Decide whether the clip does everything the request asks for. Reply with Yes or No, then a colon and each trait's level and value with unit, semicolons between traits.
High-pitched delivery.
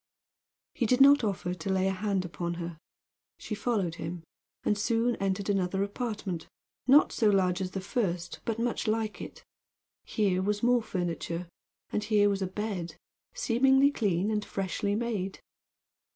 Yes: high, 200 Hz